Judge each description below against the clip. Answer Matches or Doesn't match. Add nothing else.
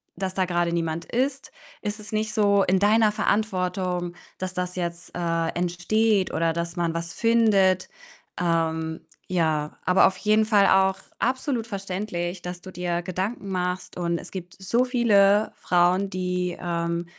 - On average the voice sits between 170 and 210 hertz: Matches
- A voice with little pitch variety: Doesn't match